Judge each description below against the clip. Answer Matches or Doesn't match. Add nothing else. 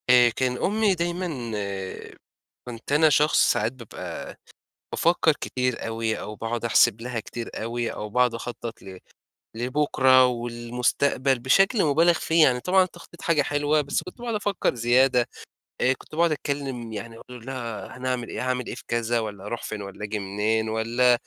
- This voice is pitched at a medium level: Doesn't match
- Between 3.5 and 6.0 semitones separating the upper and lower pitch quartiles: Matches